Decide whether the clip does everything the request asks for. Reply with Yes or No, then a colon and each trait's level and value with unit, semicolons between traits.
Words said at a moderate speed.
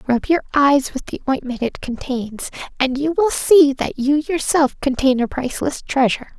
Yes: average, 180 wpm